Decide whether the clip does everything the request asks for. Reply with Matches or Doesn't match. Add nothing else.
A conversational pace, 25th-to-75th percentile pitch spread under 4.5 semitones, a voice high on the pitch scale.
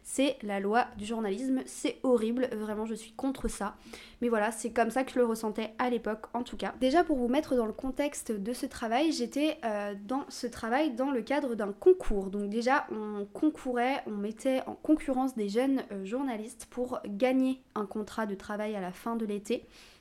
Matches